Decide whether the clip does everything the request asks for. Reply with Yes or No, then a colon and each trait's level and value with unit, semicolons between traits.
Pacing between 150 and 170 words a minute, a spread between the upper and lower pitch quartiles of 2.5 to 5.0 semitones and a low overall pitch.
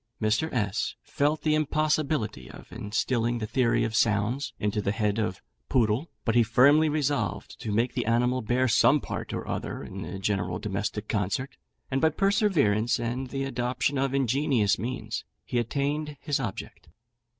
Yes: average, 160 wpm; average, 4.5 semitones; low, 120 Hz